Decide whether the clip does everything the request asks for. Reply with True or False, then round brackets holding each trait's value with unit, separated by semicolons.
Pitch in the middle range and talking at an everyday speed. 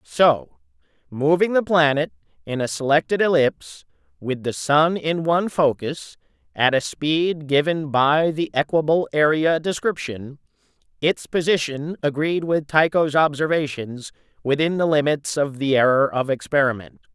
False (150 Hz; 130 wpm)